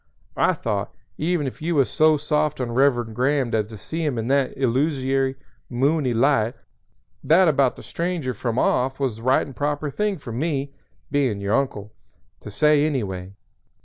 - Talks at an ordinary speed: Yes, average, 180 wpm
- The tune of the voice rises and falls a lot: No, average, 3.8 semitones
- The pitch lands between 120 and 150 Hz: Yes, low, 135 Hz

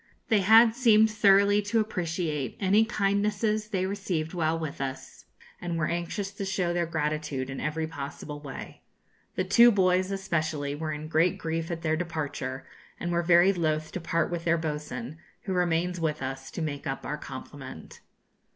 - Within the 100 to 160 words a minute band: No, average, 170 wpm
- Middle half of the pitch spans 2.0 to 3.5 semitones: No, average, 4.2 semitones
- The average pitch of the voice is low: No, medium, 170 Hz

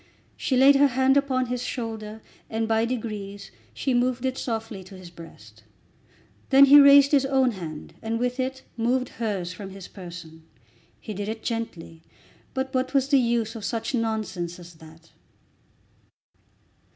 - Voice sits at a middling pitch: No, high, 225 Hz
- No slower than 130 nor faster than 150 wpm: No, average, 160 wpm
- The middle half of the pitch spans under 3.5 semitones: No, average, 5.1 semitones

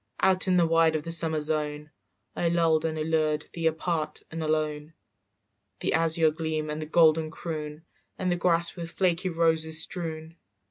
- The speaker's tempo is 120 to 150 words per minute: No, average, 175 wpm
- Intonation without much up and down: Yes, narrow, 1.3 semitones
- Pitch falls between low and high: Yes, medium, 160 Hz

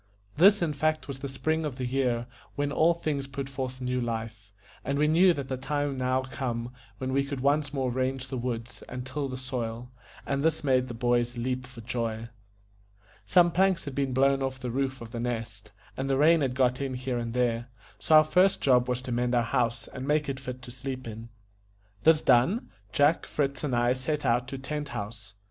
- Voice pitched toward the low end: Yes, low, 130 Hz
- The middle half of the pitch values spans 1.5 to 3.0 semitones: Yes, narrow, 2.6 semitones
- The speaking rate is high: Yes, fast, 215 wpm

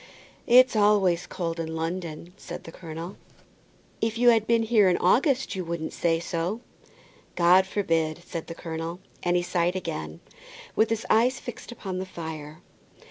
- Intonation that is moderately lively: Yes, average, 4.5 semitones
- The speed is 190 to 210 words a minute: No, average, 165 wpm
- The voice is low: No, medium, 180 Hz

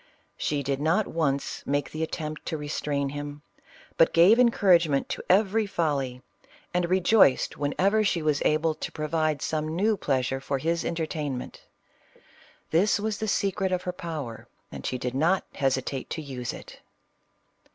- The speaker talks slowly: No, average, 165 wpm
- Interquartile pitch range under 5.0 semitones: Yes, average, 4.4 semitones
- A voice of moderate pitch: Yes, medium, 155 Hz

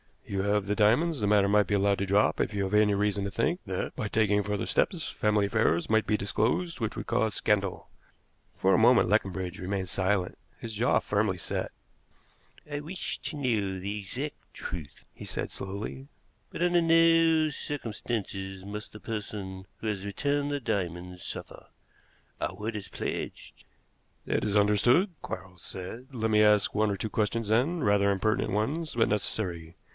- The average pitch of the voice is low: Yes, low, 105 Hz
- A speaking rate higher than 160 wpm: Yes, average, 175 wpm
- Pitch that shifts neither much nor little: Yes, average, 3.0 semitones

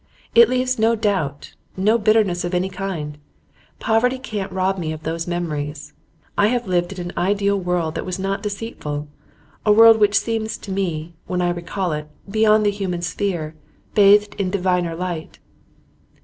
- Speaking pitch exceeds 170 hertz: Yes, high, 190 Hz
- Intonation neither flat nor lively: Yes, average, 3.3 semitones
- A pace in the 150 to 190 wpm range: Yes, average, 165 wpm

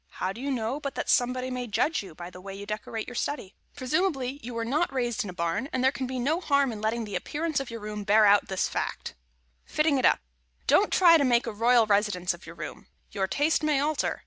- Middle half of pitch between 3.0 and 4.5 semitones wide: No, average, 5.2 semitones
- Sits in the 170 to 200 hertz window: No, high, 245 Hz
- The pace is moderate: No, fast, 255 wpm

